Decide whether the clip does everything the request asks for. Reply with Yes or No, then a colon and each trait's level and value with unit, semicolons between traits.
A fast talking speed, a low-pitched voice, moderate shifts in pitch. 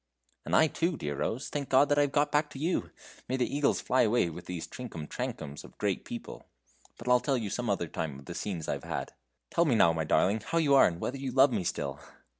No: fast, 250 wpm; low, 125 Hz; wide, 8.5 semitones